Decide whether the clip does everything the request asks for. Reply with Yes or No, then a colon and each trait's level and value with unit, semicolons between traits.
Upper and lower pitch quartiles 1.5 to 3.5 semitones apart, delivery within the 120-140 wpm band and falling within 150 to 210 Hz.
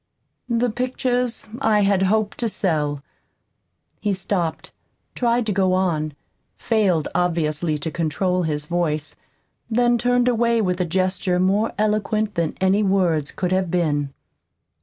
No: average, 4.7 semitones; slow, 135 wpm; high, 190 Hz